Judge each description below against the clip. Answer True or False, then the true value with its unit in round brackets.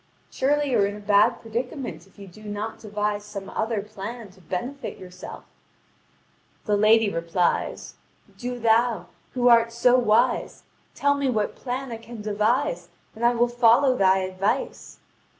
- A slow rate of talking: False (155 wpm)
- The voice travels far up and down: False (3.2 semitones)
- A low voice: False (220 Hz)